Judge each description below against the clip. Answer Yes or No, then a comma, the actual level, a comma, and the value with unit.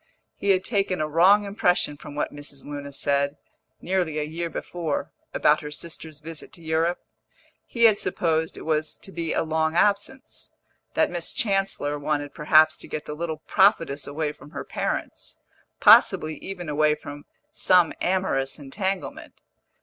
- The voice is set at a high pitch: No, medium, 160 Hz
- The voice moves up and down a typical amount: Yes, average, 3.6 semitones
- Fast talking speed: No, average, 155 wpm